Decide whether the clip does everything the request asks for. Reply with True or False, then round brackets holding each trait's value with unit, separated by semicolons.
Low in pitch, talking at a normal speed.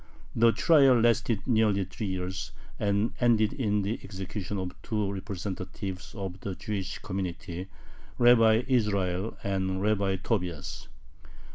False (100 Hz; 120 wpm)